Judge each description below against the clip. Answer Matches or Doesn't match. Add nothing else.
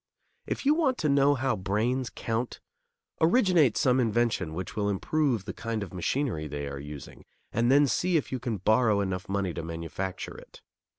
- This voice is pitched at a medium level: Doesn't match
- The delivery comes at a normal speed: Matches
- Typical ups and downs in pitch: Doesn't match